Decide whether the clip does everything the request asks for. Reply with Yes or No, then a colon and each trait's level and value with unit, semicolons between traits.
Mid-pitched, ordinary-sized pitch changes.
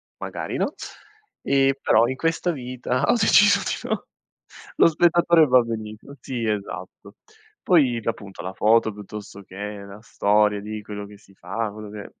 No: low, 110 Hz; average, 4.2 semitones